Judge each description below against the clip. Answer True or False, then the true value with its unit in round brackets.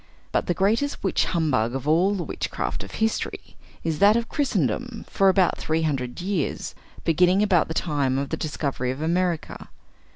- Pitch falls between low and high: True (170 Hz)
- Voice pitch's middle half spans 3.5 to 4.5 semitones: False (4.9 semitones)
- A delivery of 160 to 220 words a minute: True (170 wpm)